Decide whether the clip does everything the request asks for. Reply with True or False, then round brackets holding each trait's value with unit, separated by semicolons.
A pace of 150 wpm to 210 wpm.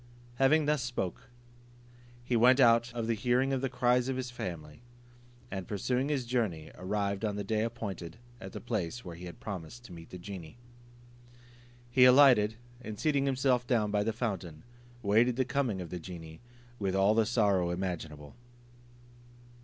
True (170 wpm)